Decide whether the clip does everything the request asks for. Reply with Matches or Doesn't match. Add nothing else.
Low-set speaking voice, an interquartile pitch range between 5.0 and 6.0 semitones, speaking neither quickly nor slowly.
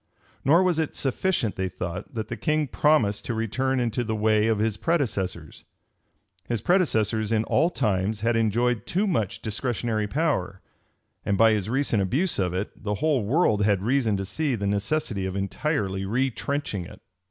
Matches